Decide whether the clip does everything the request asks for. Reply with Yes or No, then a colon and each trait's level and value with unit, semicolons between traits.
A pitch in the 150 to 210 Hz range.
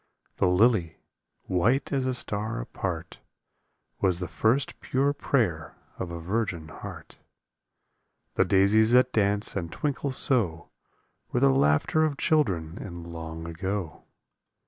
No: low, 100 Hz